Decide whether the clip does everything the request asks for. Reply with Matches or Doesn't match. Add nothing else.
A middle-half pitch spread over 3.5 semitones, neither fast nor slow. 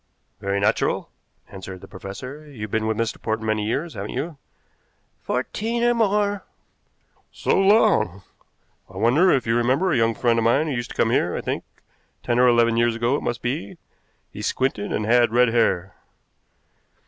Matches